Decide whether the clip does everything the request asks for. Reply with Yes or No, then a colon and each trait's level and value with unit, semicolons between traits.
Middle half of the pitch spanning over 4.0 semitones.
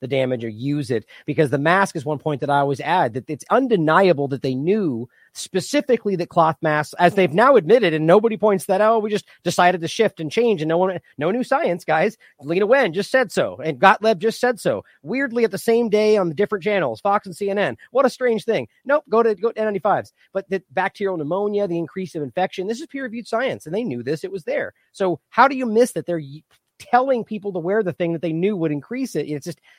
Yes: wide, 5.4 semitones